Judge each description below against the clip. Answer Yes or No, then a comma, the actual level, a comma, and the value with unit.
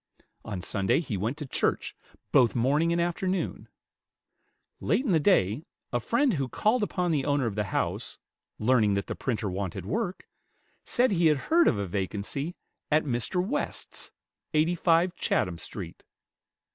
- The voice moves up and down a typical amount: No, wide, 8.8 semitones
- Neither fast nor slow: Yes, average, 155 wpm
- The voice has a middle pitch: Yes, medium, 145 Hz